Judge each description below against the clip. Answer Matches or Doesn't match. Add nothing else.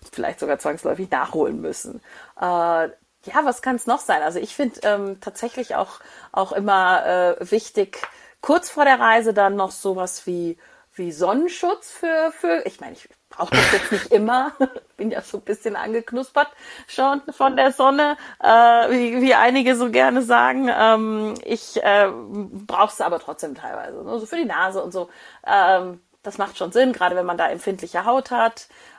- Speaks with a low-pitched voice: Doesn't match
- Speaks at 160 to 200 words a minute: Matches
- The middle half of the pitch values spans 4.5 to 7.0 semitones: Matches